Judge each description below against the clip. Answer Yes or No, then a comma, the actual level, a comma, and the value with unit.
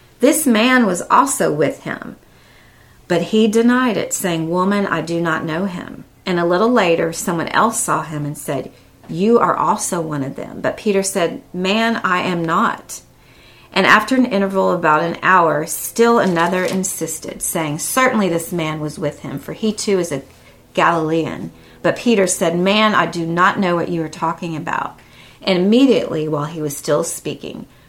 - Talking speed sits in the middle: Yes, average, 180 wpm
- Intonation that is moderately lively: Yes, average, 4.6 semitones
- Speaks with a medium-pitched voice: Yes, medium, 180 Hz